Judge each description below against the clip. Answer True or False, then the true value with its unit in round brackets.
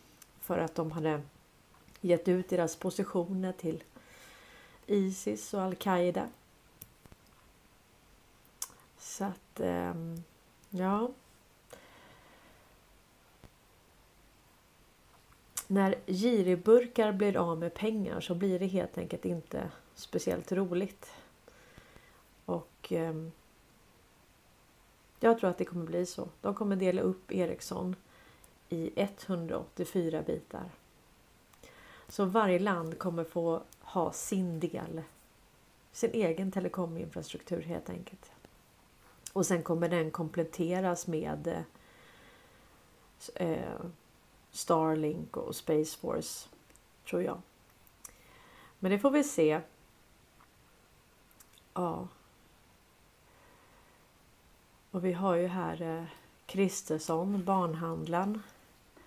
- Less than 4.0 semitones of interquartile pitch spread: True (2.8 semitones)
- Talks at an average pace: False (85 wpm)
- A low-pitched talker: False (175 Hz)